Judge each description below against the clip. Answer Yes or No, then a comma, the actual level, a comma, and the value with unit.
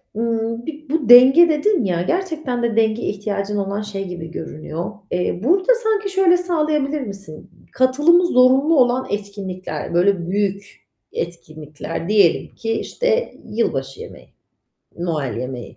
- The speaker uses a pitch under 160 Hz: No, high, 225 Hz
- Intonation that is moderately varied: No, wide, 8.8 semitones